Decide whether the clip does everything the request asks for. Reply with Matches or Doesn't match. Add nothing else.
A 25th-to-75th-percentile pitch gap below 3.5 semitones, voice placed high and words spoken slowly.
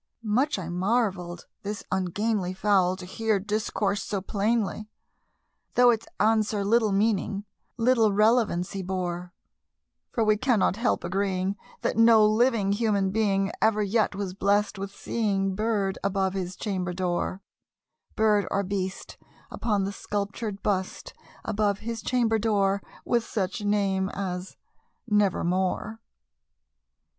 Matches